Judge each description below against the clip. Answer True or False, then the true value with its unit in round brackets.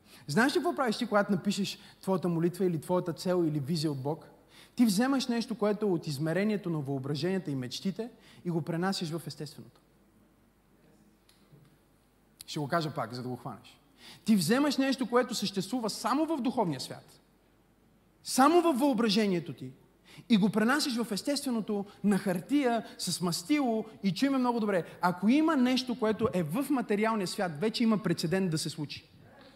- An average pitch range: False (5.7 semitones)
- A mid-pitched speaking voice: False (195 Hz)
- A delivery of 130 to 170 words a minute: True (160 wpm)